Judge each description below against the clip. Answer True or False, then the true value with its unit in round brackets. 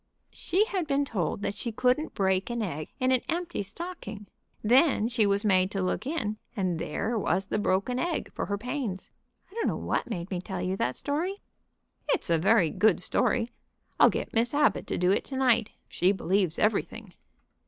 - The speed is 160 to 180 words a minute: False (190 wpm)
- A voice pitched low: False (215 Hz)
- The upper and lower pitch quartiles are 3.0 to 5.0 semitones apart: False (5.4 semitones)